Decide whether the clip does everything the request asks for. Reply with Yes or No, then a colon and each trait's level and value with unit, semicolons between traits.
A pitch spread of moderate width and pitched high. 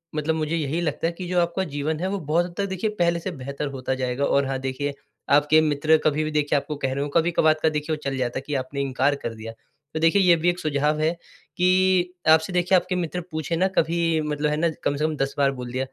No: average, 3.3 semitones; medium, 155 Hz